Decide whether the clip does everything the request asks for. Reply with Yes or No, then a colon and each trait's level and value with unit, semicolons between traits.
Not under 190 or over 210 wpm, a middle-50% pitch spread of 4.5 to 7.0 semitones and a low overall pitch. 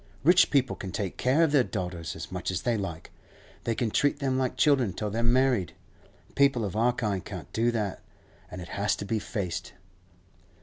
Yes: average, 200 wpm; average, 5.1 semitones; low, 115 Hz